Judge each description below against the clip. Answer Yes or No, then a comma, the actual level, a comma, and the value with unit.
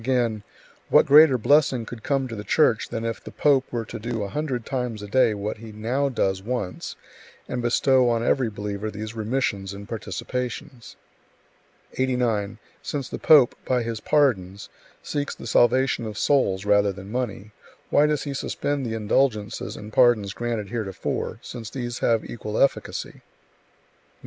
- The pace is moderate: Yes, average, 165 wpm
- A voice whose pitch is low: Yes, low, 115 Hz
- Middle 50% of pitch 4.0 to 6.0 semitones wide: No, average, 3.6 semitones